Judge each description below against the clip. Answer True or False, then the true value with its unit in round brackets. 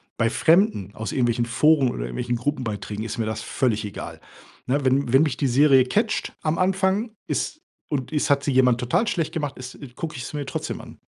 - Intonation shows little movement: False (4.7 semitones)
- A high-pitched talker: False (130 Hz)